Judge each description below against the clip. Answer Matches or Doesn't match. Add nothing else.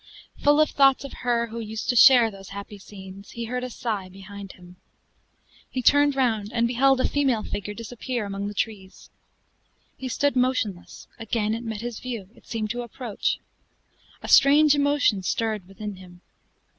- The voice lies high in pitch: Matches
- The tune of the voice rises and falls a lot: Doesn't match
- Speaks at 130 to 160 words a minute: Doesn't match